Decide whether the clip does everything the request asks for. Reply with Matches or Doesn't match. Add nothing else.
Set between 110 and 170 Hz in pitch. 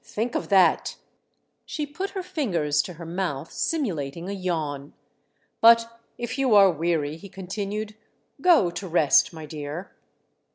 Doesn't match